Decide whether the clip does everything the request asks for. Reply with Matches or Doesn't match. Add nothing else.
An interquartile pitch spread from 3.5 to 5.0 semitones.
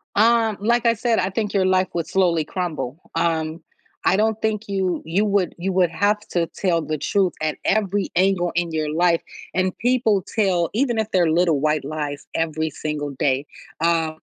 Matches